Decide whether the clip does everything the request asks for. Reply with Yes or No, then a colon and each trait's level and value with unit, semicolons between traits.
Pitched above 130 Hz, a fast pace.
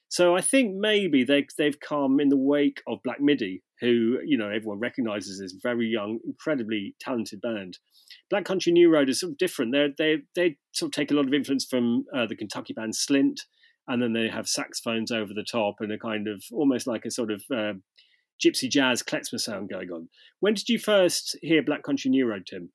Yes: medium, 140 Hz; fast, 215 wpm